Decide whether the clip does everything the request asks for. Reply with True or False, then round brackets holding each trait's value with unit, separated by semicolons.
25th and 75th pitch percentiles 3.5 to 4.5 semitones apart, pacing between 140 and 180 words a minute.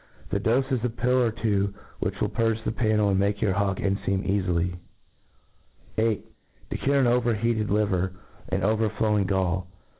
False (2.8 semitones; 160 wpm)